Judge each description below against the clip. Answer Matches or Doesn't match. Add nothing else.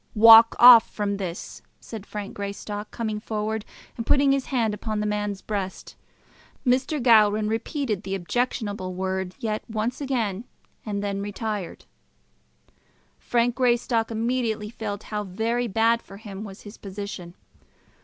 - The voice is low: Doesn't match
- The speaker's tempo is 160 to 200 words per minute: Doesn't match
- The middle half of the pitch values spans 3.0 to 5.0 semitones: Doesn't match